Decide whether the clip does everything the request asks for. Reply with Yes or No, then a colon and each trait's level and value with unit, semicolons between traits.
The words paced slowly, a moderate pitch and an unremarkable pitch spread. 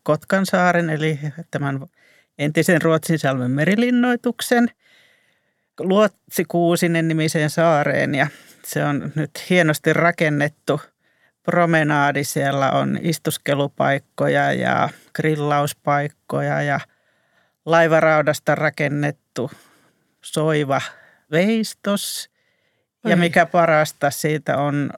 Yes: slow, 80 wpm; medium, 155 Hz; average, 3.1 semitones